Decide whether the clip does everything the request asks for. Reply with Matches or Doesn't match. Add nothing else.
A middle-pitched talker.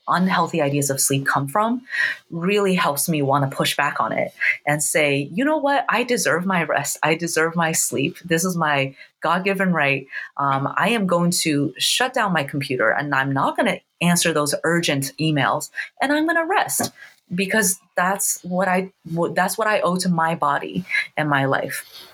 Matches